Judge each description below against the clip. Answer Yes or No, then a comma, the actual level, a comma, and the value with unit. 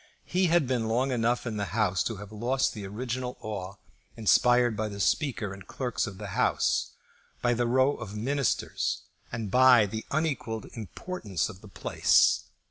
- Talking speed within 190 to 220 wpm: No, average, 175 wpm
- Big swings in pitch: No, average, 3.6 semitones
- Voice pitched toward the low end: Yes, low, 115 Hz